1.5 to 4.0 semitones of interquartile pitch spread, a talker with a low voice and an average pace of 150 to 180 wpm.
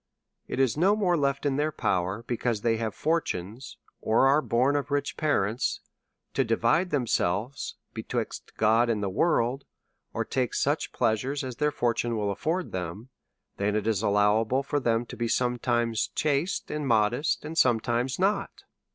No: average, 4.6 semitones; low, 120 Hz; average, 165 wpm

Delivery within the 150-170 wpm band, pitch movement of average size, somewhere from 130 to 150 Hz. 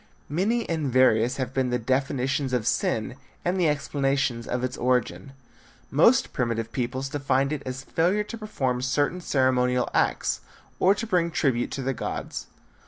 Yes: average, 160 wpm; average, 3.4 semitones; low, 135 Hz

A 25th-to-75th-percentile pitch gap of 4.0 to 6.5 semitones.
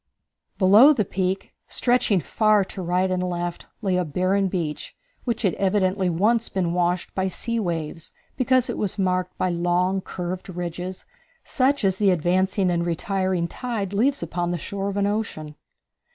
No: narrow, 2.5 semitones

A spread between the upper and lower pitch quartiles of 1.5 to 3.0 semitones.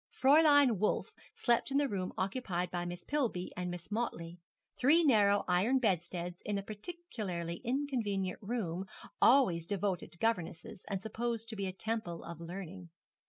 No: average, 5.2 semitones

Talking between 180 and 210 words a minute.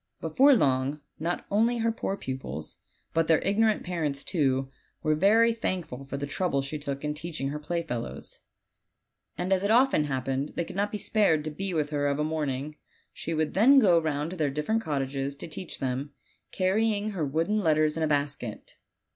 Yes: average, 190 wpm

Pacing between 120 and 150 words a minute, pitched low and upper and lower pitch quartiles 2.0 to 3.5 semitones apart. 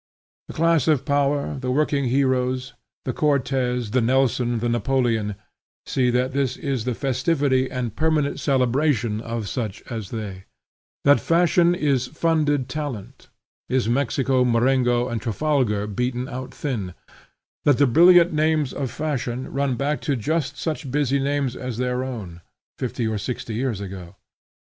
Yes: average, 145 wpm; low, 130 Hz; average, 3.2 semitones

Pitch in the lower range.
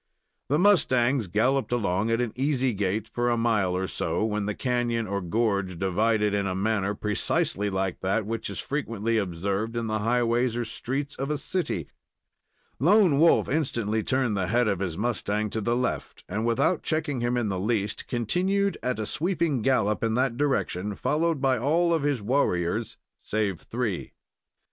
Yes: low, 115 Hz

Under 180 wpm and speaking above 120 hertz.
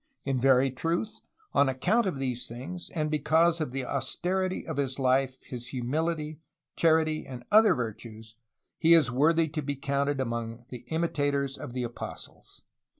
Yes: average, 155 wpm; medium, 140 Hz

